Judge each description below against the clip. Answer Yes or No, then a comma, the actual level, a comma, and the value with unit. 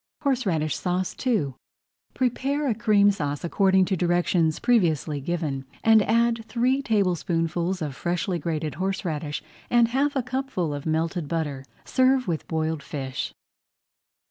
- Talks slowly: Yes, slow, 130 wpm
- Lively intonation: Yes, wide, 6.8 semitones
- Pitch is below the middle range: No, medium, 180 Hz